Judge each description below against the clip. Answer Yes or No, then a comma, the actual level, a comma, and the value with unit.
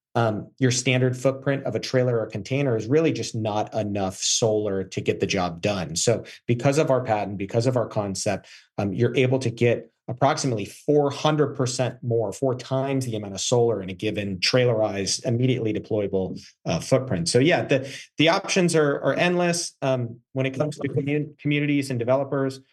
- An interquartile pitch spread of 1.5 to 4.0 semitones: No, average, 4.5 semitones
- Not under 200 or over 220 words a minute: No, average, 185 wpm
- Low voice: Yes, low, 125 Hz